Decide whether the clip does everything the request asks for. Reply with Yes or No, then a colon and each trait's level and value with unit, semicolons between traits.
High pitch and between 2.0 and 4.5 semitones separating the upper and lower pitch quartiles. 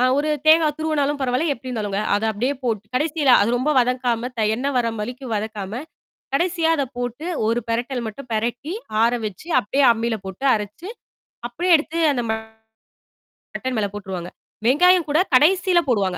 No: very high, 250 Hz; average, 5.2 semitones